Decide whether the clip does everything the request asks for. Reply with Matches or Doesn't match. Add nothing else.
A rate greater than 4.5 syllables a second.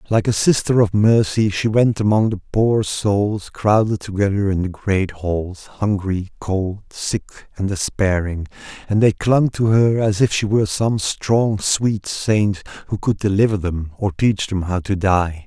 Doesn't match